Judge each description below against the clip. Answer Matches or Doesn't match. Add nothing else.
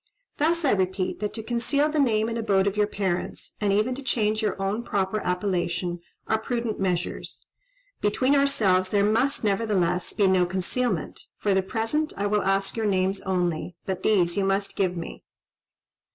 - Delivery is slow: Doesn't match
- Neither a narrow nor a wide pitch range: Matches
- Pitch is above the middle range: Matches